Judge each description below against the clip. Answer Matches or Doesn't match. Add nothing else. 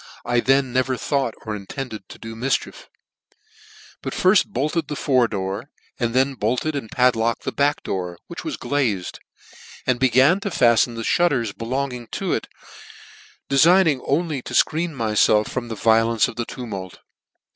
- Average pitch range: Matches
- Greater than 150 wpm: Matches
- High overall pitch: Doesn't match